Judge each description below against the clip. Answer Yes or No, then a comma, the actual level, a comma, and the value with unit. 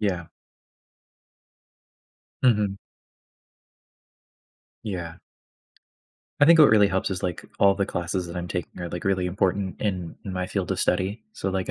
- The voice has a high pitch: No, very low, 95 Hz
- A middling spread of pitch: No, narrow, 2.2 semitones